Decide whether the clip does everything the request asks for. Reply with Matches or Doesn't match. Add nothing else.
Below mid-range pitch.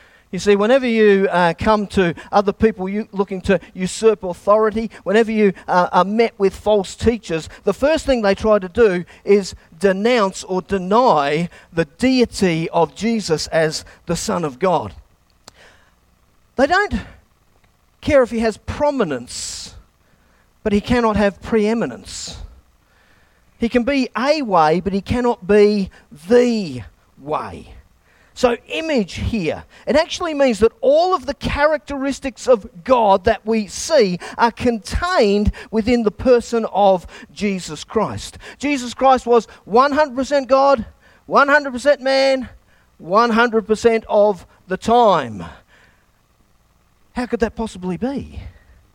Doesn't match